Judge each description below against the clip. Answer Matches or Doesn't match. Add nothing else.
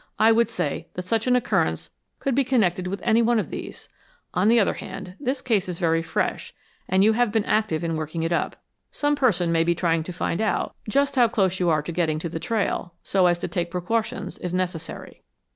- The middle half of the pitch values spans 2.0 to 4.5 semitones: Doesn't match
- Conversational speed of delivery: Doesn't match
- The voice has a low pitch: Doesn't match